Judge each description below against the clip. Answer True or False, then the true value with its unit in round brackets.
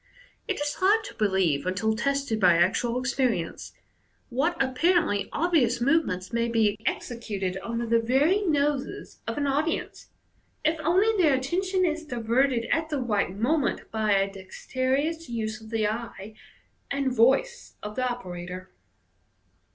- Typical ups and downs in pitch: False (5.8 semitones)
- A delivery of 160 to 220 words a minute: False (140 wpm)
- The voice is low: False (245 Hz)